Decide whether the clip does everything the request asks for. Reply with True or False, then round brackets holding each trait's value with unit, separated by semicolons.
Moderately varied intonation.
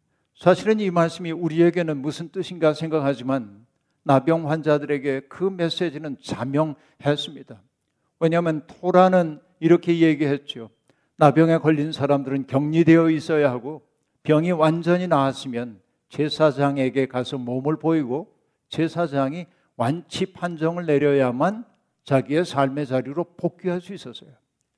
True (3.4 semitones)